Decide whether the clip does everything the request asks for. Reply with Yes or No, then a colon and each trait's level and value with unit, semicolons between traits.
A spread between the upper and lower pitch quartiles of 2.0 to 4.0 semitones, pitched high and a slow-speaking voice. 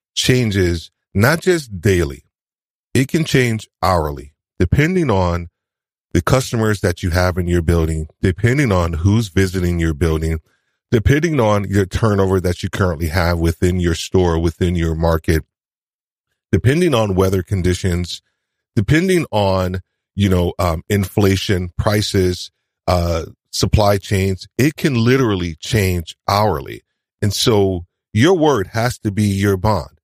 No: average, 3.7 semitones; very low, 95 Hz; slow, 130 wpm